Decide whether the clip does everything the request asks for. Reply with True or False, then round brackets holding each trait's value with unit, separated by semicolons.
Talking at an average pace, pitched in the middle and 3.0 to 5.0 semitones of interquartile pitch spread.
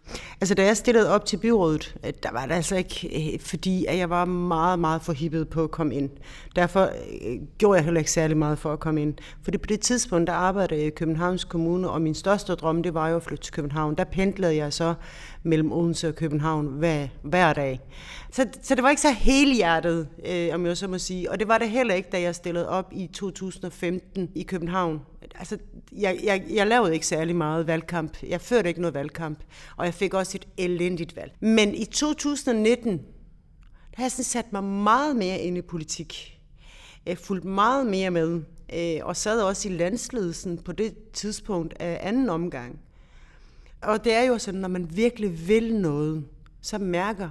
True (200 wpm; 175 Hz; 3.7 semitones)